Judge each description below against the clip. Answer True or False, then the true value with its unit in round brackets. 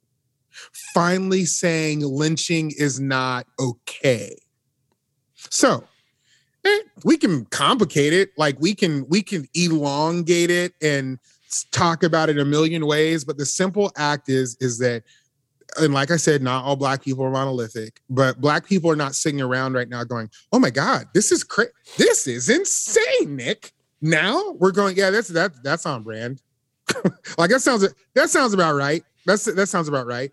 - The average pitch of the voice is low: False (155 Hz)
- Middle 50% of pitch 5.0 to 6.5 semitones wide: True (5.4 semitones)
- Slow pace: False (165 wpm)